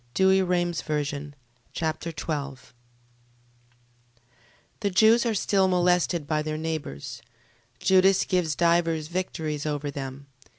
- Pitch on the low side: No, medium, 160 Hz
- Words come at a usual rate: No, slow, 100 wpm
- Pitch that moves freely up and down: No, average, 3.7 semitones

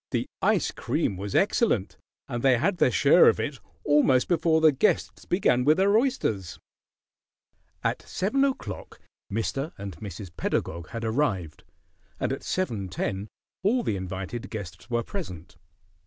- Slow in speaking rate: No, average, 145 wpm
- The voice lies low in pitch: Yes, low, 120 Hz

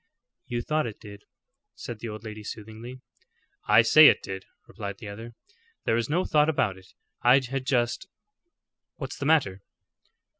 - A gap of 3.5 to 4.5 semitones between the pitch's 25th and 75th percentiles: Yes, average, 4.1 semitones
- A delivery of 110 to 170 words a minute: Yes, average, 160 wpm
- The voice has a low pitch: Yes, low, 115 Hz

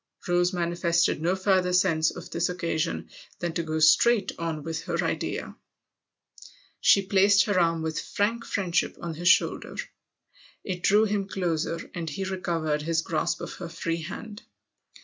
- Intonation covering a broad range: No, narrow, 2.6 semitones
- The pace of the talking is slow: No, average, 155 wpm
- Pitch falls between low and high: Yes, medium, 175 Hz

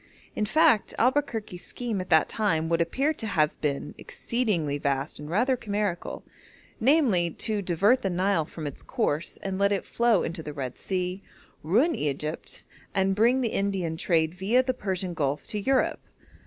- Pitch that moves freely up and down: Yes, wide, 5.8 semitones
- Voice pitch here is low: No, high, 190 Hz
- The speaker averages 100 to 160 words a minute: No, average, 170 wpm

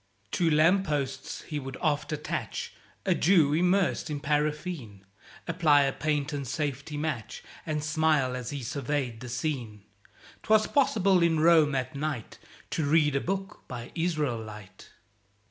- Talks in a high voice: No, medium, 150 Hz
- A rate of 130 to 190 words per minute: Yes, average, 140 wpm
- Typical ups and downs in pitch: Yes, average, 3.4 semitones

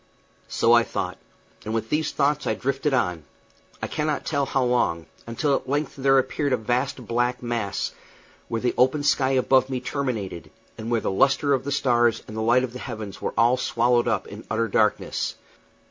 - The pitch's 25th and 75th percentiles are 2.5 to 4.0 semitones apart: Yes, average, 3.0 semitones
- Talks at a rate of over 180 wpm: Yes, average, 190 wpm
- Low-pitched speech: Yes, low, 125 Hz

